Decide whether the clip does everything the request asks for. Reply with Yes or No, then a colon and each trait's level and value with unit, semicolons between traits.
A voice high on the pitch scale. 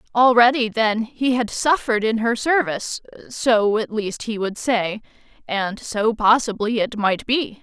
Yes: high, 225 Hz